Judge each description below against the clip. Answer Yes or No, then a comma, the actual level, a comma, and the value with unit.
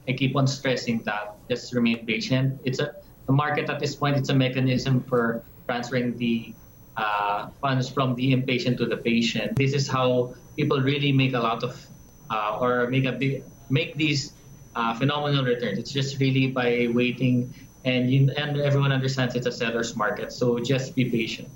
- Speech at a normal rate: Yes, average, 185 wpm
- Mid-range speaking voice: No, low, 130 Hz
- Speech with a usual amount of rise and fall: No, narrow, 2.2 semitones